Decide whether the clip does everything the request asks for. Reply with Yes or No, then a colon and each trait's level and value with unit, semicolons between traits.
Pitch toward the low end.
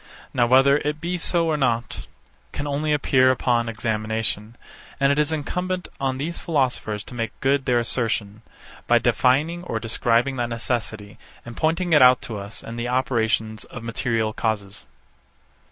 Yes: low, 125 Hz